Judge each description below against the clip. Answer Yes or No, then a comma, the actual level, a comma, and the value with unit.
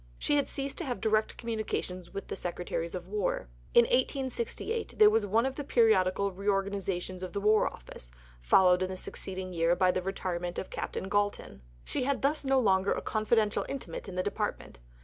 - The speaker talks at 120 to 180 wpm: No, average, 190 wpm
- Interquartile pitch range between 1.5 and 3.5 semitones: No, average, 4.2 semitones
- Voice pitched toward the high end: Yes, high, 200 Hz